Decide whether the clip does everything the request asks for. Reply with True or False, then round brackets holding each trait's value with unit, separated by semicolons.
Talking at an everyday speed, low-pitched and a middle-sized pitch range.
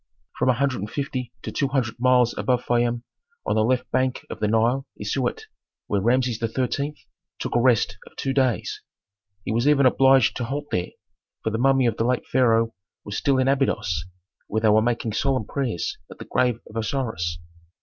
True (195 wpm; 120 Hz; 3.0 semitones)